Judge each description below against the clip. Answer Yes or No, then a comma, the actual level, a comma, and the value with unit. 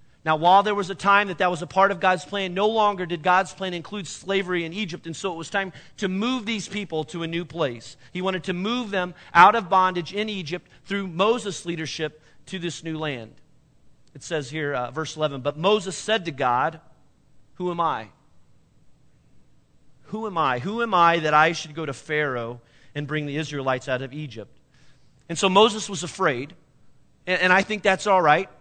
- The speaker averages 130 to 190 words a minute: No, fast, 205 wpm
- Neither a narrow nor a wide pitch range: Yes, average, 4.7 semitones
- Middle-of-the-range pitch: Yes, medium, 170 Hz